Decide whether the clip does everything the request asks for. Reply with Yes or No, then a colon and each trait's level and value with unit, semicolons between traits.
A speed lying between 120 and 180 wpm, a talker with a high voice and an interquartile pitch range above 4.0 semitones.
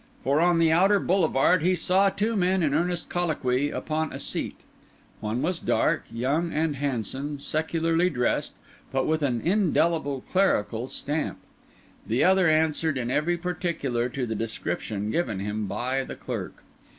No: average, 150 wpm; medium, 155 Hz; average, 5.3 semitones